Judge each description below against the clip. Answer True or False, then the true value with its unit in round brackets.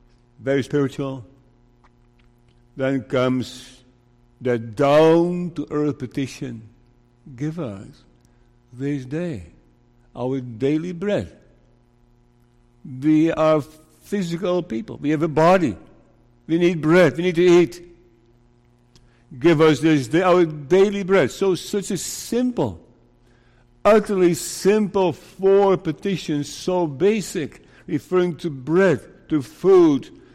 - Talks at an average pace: False (105 wpm)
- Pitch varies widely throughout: True (6.4 semitones)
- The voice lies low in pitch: False (145 Hz)